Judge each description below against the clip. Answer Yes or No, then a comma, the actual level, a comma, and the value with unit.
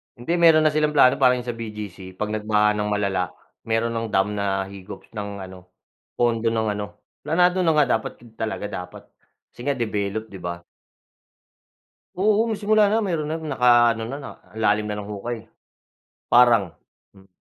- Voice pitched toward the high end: No, low, 110 Hz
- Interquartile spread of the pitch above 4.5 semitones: Yes, average, 4.9 semitones